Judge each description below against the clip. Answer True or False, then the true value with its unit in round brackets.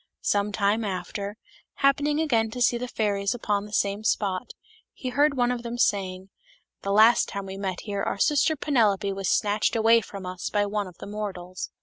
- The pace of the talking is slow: False (200 wpm)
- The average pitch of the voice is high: True (210 Hz)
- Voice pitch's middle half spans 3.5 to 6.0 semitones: False (3.1 semitones)